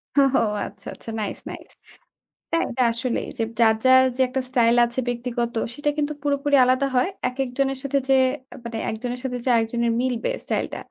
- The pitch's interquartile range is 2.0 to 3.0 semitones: Yes, narrow, 2.4 semitones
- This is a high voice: Yes, very high, 250 Hz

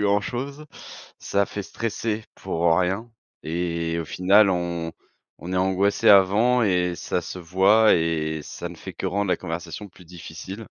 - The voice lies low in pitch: Yes, very low, 95 Hz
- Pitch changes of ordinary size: Yes, average, 3.1 semitones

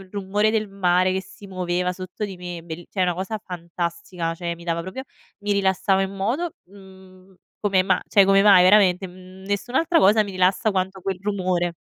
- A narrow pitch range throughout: Yes, narrow, 1.8 semitones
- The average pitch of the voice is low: No, high, 190 Hz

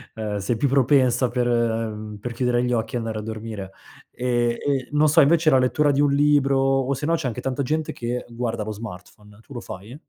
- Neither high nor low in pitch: No, low, 125 Hz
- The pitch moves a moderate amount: Yes, average, 3.6 semitones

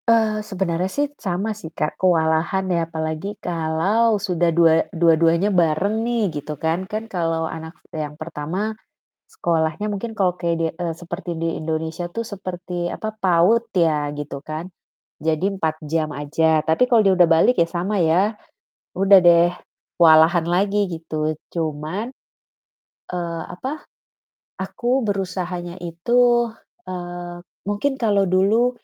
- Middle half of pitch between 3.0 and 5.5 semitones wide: Yes, average, 3.8 semitones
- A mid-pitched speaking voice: Yes, medium, 175 Hz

